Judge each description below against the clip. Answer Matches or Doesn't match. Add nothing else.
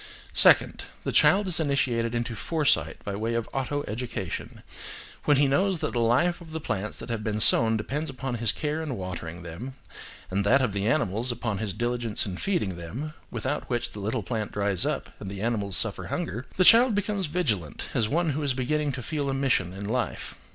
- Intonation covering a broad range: Matches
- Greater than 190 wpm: Matches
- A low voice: Matches